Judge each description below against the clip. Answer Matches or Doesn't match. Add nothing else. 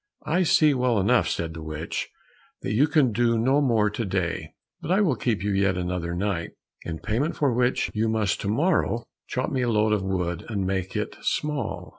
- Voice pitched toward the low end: Matches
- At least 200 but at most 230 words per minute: Matches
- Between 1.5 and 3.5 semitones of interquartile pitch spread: Doesn't match